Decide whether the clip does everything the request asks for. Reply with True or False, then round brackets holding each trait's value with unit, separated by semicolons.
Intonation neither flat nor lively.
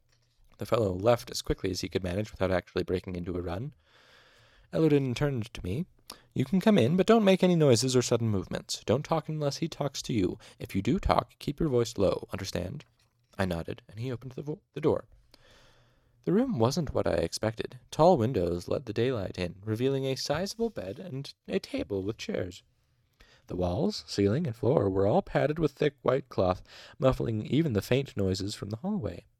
False (6.1 semitones)